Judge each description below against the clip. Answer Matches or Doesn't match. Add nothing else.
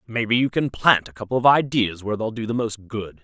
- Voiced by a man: Matches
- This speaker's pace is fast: Matches